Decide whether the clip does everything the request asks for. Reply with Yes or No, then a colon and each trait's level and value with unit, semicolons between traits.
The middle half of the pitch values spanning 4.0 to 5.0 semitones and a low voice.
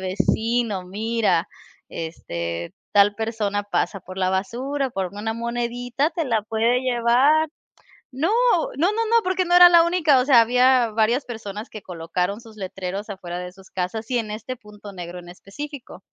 No: average, 4.7 semitones; high, 225 Hz